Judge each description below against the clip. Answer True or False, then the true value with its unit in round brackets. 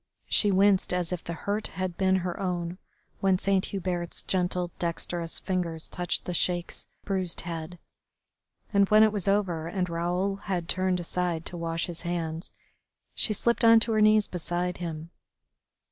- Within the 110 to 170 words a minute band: True (160 wpm)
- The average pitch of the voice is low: False (180 Hz)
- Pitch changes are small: True (2.3 semitones)